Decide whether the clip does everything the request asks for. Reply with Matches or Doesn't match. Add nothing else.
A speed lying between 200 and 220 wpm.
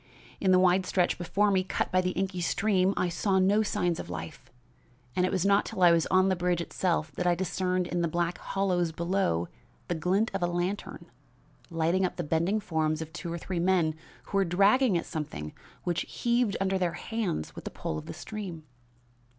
Matches